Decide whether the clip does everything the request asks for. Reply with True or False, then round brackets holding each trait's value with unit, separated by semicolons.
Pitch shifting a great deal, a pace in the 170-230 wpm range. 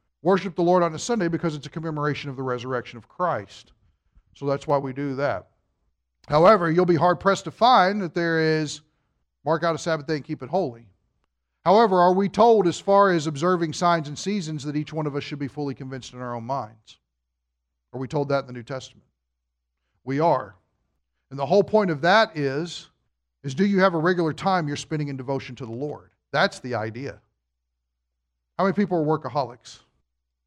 True (7.7 semitones; 205 wpm)